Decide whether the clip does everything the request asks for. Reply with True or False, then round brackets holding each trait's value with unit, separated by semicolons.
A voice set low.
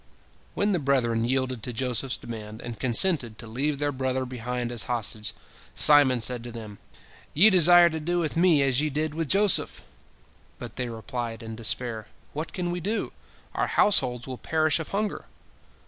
True (130 Hz)